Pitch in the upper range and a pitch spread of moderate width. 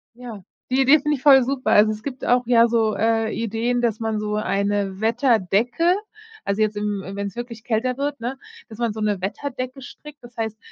Yes: high, 230 Hz; average, 3.1 semitones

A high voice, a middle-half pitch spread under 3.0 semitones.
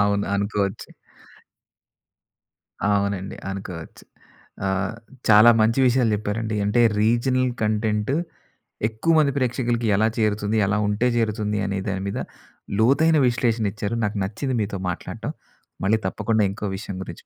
No: low, 110 Hz; narrow, 2.5 semitones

